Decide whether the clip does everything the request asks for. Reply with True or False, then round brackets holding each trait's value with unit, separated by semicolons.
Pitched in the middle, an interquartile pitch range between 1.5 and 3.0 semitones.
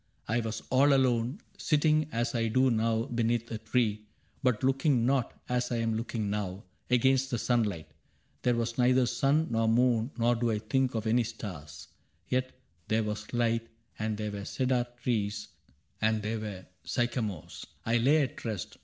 False (115 Hz; 2.5 semitones)